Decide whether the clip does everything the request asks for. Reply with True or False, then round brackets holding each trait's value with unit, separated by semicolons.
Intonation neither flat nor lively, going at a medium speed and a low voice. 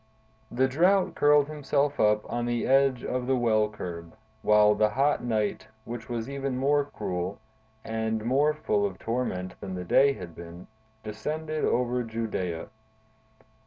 True (4.6 semitones; 150 wpm; 120 Hz)